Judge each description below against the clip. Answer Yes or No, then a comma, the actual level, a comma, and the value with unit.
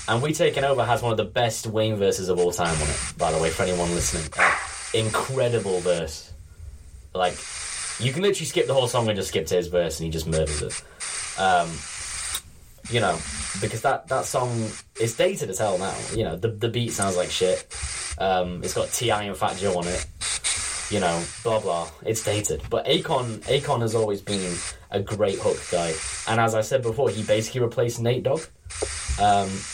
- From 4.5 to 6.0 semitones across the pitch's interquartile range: Yes, average, 5.3 semitones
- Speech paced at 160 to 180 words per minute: No, average, 200 wpm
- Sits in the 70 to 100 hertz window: Yes, very low, 95 Hz